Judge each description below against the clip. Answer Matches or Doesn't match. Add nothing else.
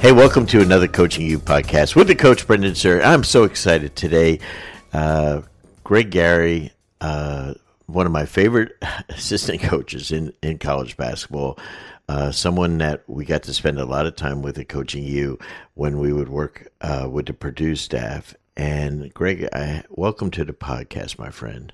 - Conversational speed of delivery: Matches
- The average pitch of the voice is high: Doesn't match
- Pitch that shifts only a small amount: Doesn't match